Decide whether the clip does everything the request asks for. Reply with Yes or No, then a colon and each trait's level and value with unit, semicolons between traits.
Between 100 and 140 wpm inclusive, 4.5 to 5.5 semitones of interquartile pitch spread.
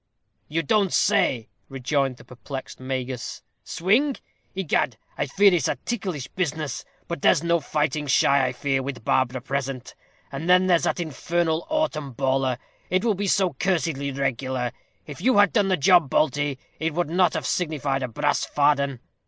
No: average, 165 wpm; average, 4.9 semitones